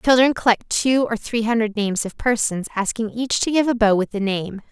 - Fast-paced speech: Yes, fast, 230 wpm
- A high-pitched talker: Yes, high, 225 Hz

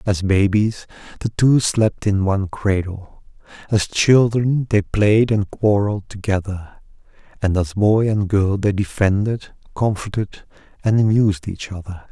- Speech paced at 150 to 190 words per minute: No, slow, 135 wpm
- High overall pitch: No, low, 100 Hz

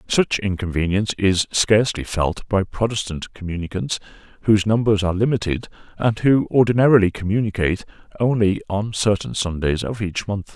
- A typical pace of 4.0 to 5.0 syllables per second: No, 5.5 syllables/s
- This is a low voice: Yes, low, 100 Hz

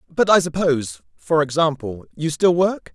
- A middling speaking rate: Yes, average, 165 wpm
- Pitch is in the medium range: Yes, medium, 150 Hz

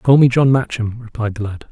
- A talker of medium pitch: No, low, 120 Hz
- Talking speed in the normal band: No, fast, 245 wpm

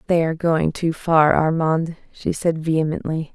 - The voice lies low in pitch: No, medium, 160 Hz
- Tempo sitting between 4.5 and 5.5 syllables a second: Yes, 4.7 syllables/s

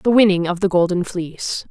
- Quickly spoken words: Yes, fast, 210 wpm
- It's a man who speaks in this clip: No, female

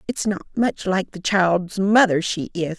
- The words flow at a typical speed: Yes, average, 195 wpm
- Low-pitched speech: No, high, 190 Hz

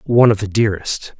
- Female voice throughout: No, male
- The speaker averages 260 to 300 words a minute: No, average, 200 wpm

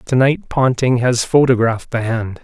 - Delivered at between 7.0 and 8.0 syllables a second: No, 4.7 syllables/s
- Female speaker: No, male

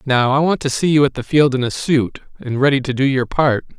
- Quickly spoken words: Yes, fast, 285 wpm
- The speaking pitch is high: No, low, 135 Hz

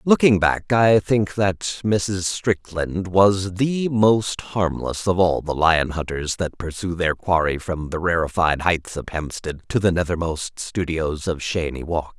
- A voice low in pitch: Yes, very low, 90 Hz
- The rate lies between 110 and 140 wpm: No, average, 160 wpm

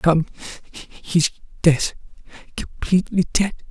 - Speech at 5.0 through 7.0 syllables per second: No, 3.5 syllables/s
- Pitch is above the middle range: No, medium, 170 Hz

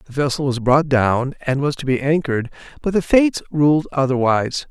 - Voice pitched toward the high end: No, medium, 140 Hz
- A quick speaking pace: No, average, 190 wpm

